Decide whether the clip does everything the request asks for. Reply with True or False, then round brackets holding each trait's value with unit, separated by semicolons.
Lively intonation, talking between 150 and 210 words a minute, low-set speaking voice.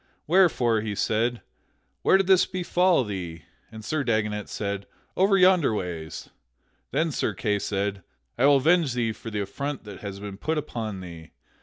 True (7.5 semitones; 165 wpm; 110 Hz)